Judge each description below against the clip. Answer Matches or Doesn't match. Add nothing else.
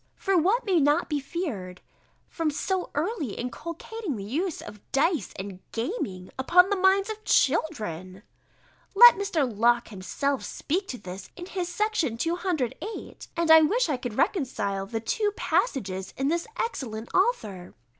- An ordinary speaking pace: Matches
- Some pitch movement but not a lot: Doesn't match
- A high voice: Matches